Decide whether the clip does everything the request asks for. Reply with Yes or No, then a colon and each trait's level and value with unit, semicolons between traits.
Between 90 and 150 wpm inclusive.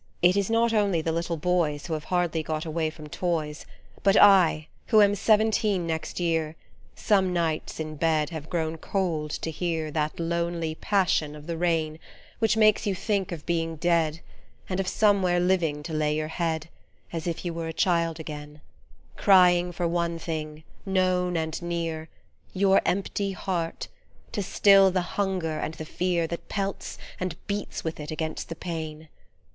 No: average, 170 wpm